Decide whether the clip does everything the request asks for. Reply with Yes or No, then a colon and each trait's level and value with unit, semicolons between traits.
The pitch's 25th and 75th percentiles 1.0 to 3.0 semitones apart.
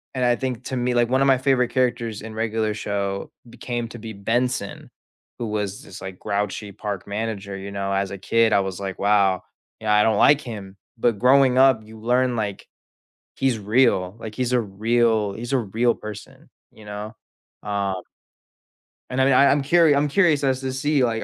No: average, 3.8 semitones